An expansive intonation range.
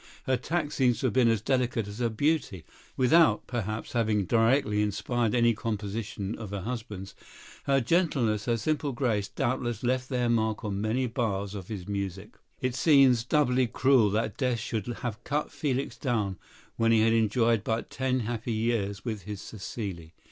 No: average, 3.3 semitones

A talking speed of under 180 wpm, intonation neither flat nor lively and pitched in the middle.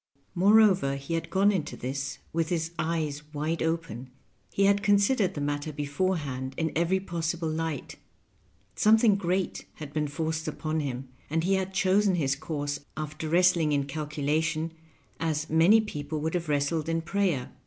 Yes: average, 160 wpm; average, 3.6 semitones; medium, 160 Hz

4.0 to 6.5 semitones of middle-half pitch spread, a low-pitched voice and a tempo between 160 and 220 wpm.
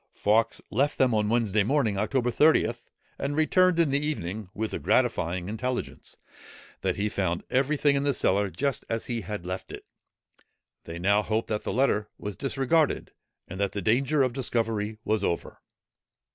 Yes: average, 4.9 semitones; low, 115 Hz; average, 175 wpm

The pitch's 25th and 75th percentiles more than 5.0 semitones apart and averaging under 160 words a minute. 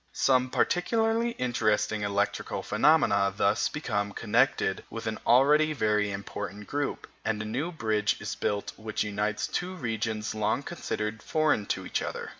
Yes: wide, 5.6 semitones; average, 145 wpm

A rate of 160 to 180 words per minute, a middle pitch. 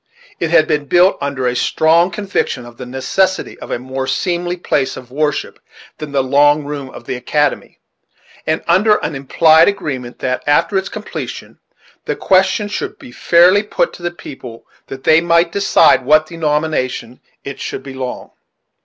Yes: average, 170 wpm; medium, 150 Hz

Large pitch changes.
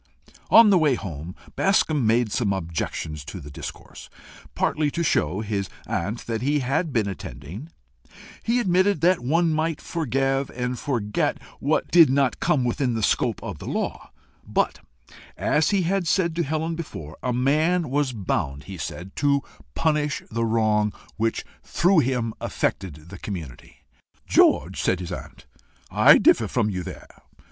Yes: wide, 7.9 semitones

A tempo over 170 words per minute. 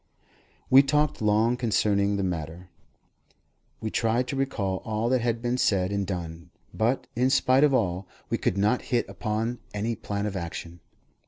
No: average, 165 wpm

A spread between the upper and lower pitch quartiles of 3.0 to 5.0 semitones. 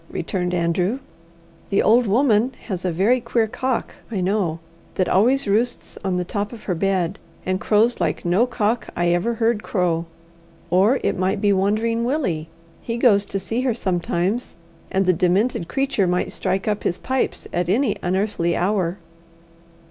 Yes: average, 4.3 semitones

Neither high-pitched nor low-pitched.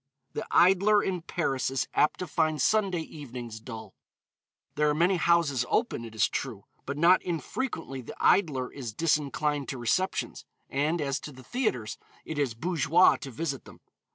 Yes: medium, 150 Hz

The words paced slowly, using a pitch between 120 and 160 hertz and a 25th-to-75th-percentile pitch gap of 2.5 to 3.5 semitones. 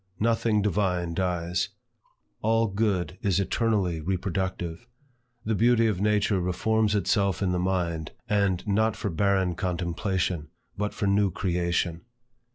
No: slow, 125 wpm; very low, 95 Hz; average, 2.9 semitones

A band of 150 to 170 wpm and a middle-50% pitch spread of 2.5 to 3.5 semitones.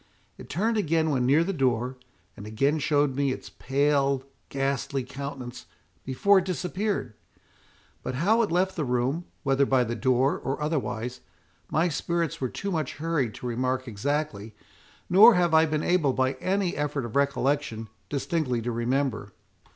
No: average, 160 wpm; average, 4.3 semitones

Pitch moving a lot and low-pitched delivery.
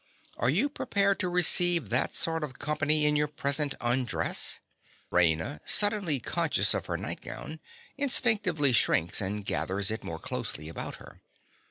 No: wide, 8.2 semitones; medium, 150 Hz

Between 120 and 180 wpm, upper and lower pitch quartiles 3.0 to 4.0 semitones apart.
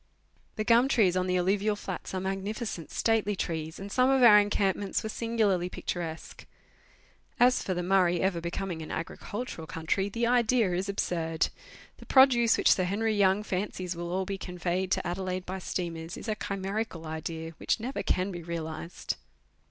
Yes: average, 170 wpm; average, 3.4 semitones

